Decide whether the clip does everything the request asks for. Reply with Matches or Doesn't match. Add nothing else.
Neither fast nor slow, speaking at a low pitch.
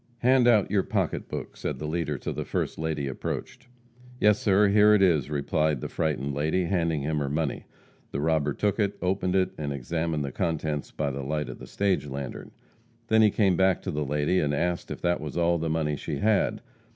Doesn't match